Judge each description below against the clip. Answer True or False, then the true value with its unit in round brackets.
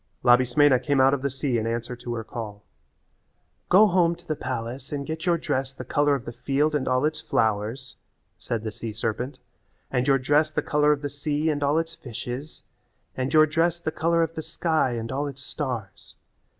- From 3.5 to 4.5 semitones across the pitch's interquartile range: True (4.1 semitones)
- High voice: False (140 Hz)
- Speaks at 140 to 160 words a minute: False (205 wpm)